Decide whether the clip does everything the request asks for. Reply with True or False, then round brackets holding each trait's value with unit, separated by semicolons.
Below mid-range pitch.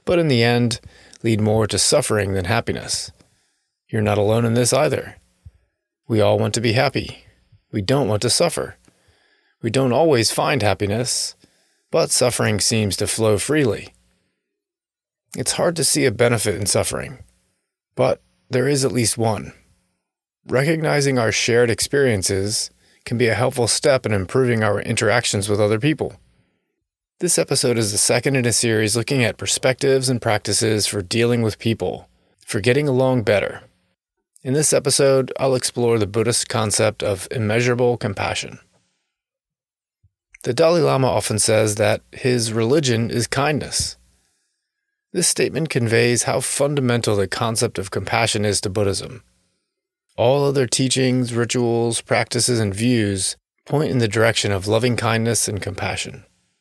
True (115 Hz)